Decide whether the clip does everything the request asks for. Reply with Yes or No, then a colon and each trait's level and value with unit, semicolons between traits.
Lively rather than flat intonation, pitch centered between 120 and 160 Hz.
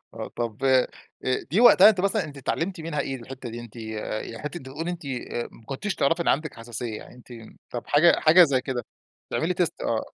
Yes: wide, 5.8 semitones; low, 135 Hz